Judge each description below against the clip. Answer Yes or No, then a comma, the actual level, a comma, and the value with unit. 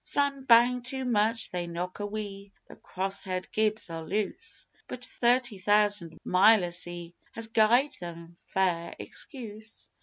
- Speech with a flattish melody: No, average, 4.4 semitones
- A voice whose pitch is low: No, high, 205 Hz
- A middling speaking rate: Yes, average, 145 wpm